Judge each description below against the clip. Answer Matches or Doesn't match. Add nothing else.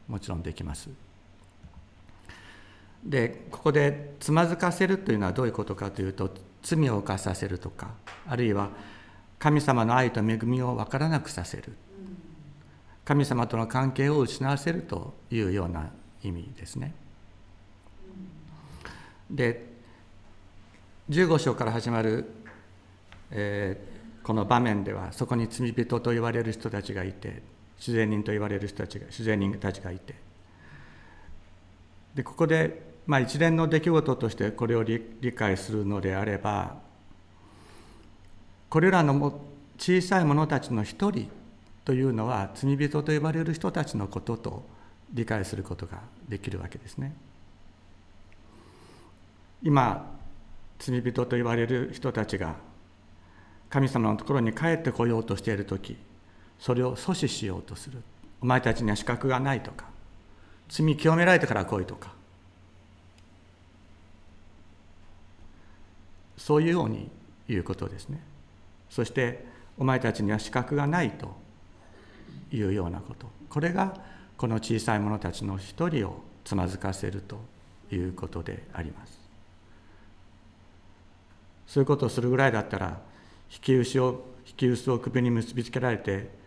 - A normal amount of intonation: Matches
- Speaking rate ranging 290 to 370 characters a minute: Doesn't match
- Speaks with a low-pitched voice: Matches